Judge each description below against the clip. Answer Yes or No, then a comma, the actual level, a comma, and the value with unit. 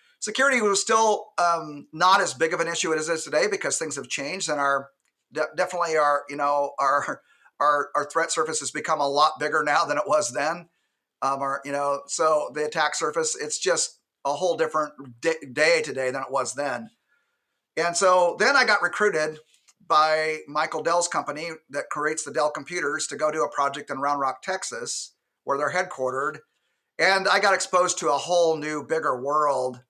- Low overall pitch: No, medium, 155 Hz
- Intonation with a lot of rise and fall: No, average, 4.8 semitones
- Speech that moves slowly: No, average, 195 wpm